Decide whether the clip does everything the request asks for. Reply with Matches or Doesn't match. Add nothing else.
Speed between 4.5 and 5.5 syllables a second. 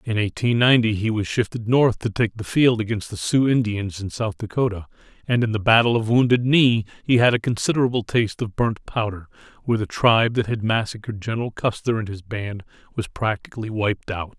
Doesn't match